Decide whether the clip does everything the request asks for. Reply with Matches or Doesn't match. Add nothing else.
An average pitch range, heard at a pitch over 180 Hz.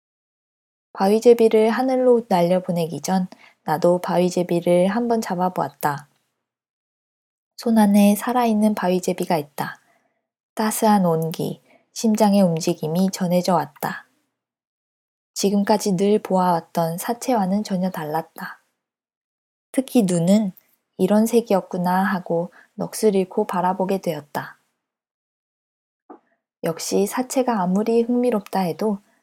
Matches